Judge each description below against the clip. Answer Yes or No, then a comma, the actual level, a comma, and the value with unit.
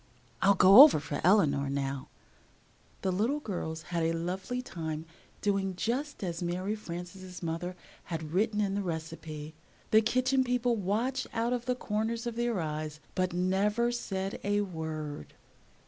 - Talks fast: No, average, 150 wpm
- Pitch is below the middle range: No, high, 190 Hz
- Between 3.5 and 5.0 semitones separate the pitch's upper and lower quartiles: No, wide, 5.6 semitones